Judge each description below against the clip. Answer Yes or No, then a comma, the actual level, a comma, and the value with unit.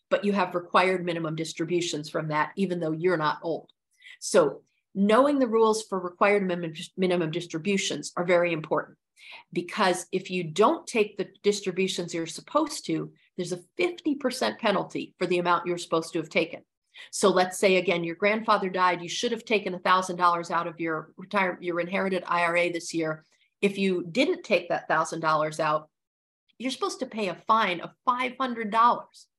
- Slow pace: No, average, 165 wpm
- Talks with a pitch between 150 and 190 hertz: Yes, medium, 185 Hz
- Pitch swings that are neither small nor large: Yes, average, 3.8 semitones